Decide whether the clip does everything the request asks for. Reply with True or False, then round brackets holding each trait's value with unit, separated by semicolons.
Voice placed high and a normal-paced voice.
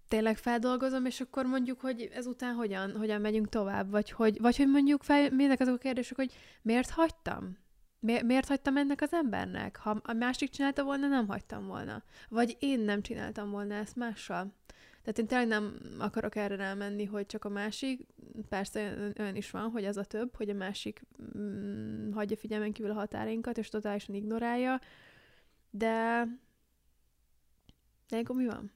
False (225 Hz; 165 wpm)